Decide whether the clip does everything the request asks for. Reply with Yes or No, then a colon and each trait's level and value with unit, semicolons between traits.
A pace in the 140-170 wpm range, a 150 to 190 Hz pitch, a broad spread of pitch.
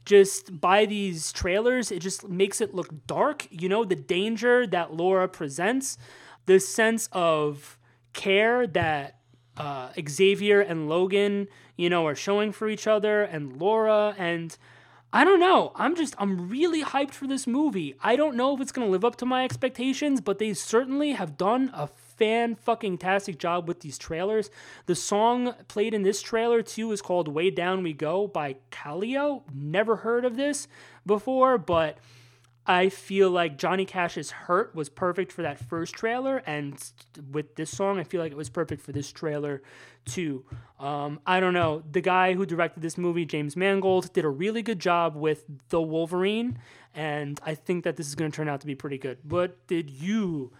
No: average, 185 wpm; medium, 185 Hz; wide, 5.7 semitones